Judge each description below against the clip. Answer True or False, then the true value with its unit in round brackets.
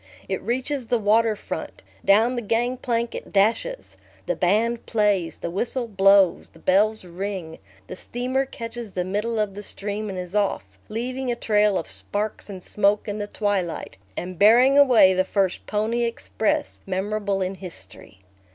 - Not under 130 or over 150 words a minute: False (165 wpm)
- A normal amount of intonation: True (3.3 semitones)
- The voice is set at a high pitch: True (210 Hz)